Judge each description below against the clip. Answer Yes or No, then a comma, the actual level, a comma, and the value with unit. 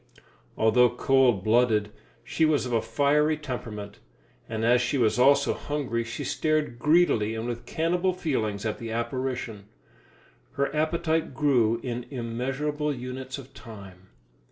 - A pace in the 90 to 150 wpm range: Yes, slow, 135 wpm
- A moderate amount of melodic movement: Yes, average, 4.5 semitones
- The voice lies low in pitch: Yes, low, 125 Hz